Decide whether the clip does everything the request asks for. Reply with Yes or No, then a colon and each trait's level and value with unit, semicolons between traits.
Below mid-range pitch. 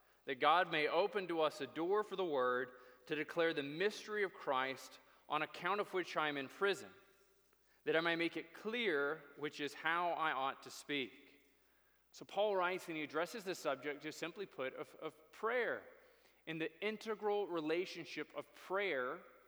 No: medium, 160 Hz